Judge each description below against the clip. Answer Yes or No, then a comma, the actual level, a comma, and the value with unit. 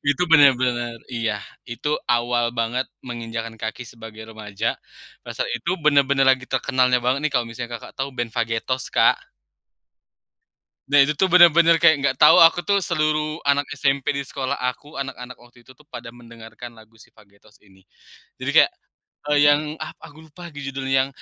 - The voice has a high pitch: No, low, 130 Hz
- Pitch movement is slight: No, average, 3.7 semitones